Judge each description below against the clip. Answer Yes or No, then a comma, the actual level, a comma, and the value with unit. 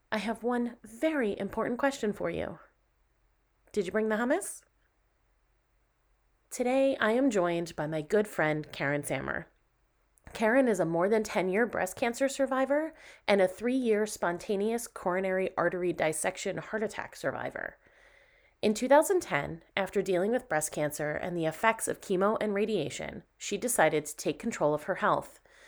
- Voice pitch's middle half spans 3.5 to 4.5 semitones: No, wide, 5.4 semitones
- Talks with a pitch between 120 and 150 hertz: No, high, 210 Hz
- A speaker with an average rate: Yes, average, 155 wpm